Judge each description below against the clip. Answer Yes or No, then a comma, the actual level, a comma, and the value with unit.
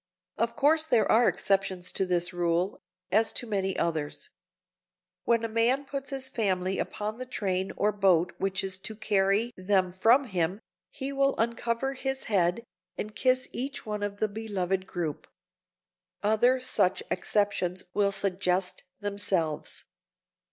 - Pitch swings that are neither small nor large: Yes, average, 4.0 semitones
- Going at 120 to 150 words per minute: Yes, average, 145 wpm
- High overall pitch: Yes, high, 205 Hz